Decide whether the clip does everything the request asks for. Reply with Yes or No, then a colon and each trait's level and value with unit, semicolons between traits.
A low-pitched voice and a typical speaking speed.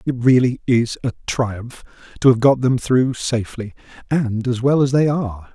Yes: low, 125 Hz; average, 185 wpm